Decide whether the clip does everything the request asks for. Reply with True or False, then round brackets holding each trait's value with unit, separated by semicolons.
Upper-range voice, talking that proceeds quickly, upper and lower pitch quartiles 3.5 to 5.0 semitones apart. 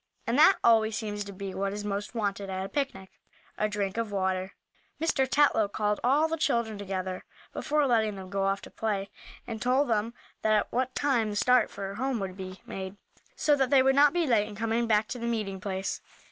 True (215 Hz; 215 wpm; 4.1 semitones)